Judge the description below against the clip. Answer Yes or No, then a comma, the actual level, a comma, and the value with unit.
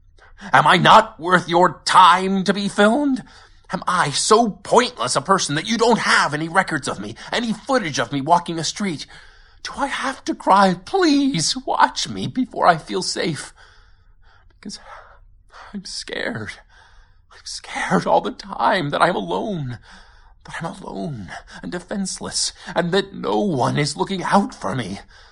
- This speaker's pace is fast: No, average, 160 wpm